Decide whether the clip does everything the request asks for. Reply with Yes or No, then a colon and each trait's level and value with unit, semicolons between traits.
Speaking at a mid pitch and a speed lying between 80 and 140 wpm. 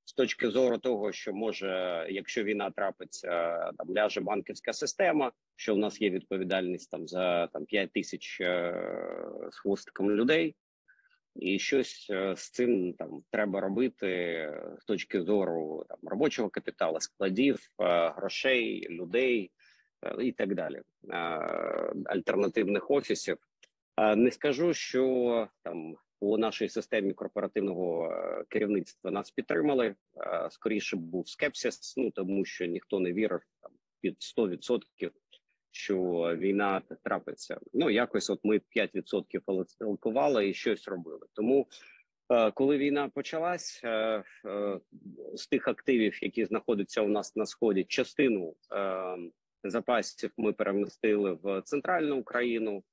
No: low, 100 Hz; average, 120 wpm